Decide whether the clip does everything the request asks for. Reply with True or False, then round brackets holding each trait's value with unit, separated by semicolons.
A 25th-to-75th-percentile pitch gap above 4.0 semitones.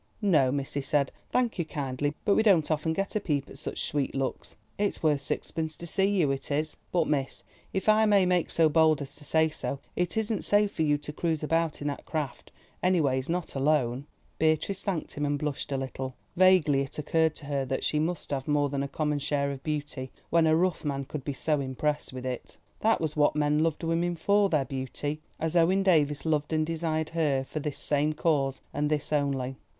False (2.8 semitones)